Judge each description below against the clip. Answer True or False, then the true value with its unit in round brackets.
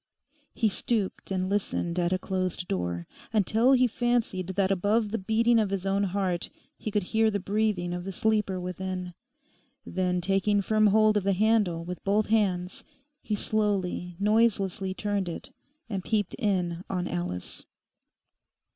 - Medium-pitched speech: False (195 Hz)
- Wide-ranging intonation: False (2.9 semitones)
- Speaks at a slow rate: False (155 wpm)